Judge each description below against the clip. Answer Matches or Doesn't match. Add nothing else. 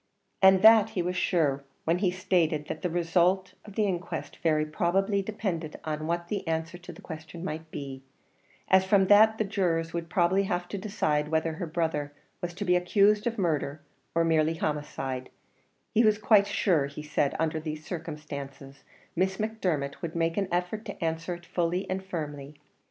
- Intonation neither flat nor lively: Matches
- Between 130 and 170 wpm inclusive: Doesn't match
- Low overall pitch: Doesn't match